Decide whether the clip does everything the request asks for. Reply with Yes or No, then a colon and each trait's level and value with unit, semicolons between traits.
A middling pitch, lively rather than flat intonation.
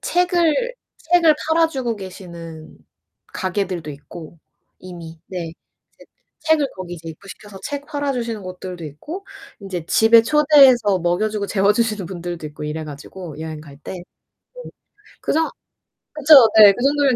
No: high, 195 Hz; wide, 8.8 semitones